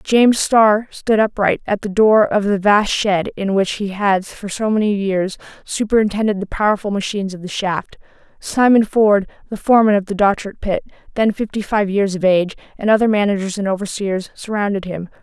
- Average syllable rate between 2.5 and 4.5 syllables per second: No, 5.3 syllables/s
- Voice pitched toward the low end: No, high, 205 Hz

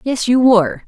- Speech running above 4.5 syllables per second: Yes, 5.3 syllables/s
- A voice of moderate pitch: No, high, 225 Hz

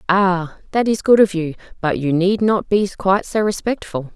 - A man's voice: No, female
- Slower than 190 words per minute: No, average, 200 wpm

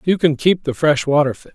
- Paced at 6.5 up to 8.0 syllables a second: No, 5.5 syllables/s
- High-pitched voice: No, medium, 150 Hz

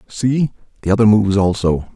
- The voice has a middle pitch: No, low, 105 Hz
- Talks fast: No, average, 155 wpm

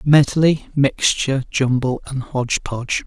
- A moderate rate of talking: No, slow, 115 wpm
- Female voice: No, male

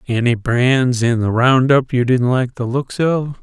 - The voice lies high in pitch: No, low, 125 Hz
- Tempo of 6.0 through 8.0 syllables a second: No, 4.0 syllables/s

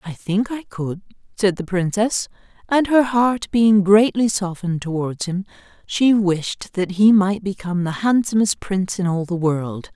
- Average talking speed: Yes, average, 170 wpm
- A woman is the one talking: Yes, female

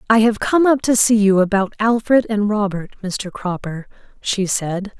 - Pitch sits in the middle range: No, high, 210 Hz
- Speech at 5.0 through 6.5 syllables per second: No, 4.4 syllables/s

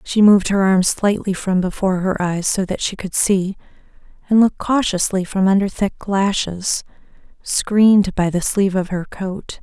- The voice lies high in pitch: Yes, high, 195 Hz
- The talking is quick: No, average, 175 wpm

